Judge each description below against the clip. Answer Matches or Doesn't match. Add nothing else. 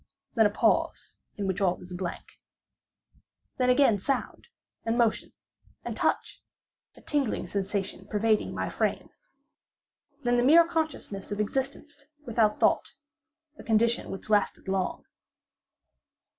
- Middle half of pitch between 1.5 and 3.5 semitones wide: Doesn't match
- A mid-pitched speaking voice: Doesn't match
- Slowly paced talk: Matches